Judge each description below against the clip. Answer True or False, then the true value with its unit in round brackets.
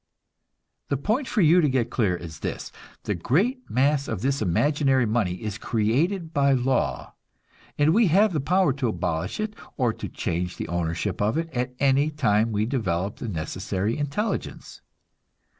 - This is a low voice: True (130 Hz)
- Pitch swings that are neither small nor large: False (6.7 semitones)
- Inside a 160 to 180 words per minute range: True (165 wpm)